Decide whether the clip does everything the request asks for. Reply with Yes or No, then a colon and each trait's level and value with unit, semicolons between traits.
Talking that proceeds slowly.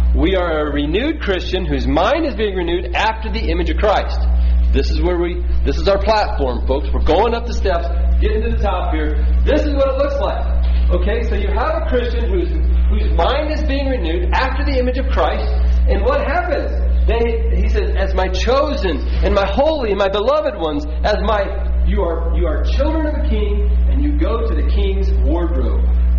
No: fast, 205 wpm